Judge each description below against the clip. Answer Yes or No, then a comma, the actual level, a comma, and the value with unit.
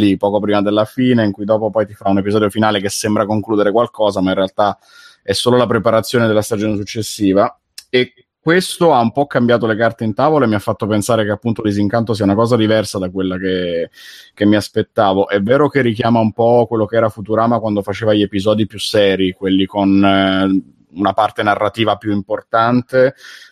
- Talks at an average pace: No, fast, 200 wpm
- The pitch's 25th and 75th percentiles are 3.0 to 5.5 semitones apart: No, narrow, 2.4 semitones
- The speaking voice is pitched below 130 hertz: Yes, low, 110 Hz